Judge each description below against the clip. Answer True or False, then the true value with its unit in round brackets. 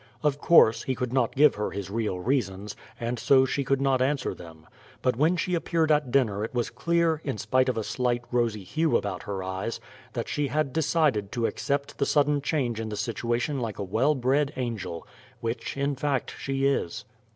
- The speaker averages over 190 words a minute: True (200 wpm)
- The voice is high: False (130 Hz)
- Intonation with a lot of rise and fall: False (4.3 semitones)